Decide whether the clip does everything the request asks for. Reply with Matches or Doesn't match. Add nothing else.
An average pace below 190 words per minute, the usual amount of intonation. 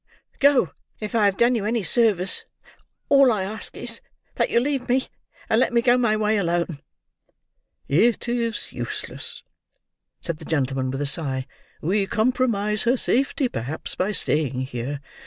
Doesn't match